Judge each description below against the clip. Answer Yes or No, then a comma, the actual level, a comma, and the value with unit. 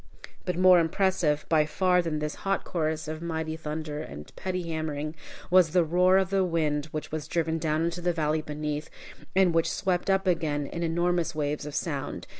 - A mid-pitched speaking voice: Yes, medium, 160 Hz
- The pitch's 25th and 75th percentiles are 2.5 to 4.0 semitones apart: Yes, average, 2.8 semitones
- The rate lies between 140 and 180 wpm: No, average, 190 wpm